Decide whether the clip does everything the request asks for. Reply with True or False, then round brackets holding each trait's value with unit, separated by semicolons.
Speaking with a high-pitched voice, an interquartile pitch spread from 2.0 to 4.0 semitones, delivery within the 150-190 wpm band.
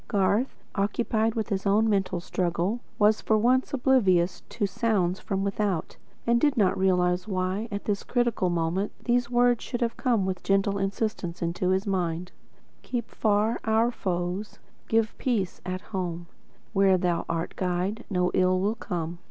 True (195 Hz; 3.5 semitones; 160 wpm)